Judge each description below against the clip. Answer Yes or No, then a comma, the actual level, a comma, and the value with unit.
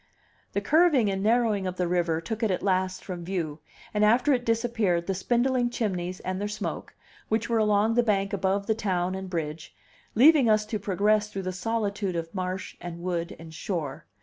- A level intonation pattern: No, average, 3.6 semitones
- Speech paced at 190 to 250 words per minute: Yes, average, 200 wpm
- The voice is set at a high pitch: Yes, high, 200 Hz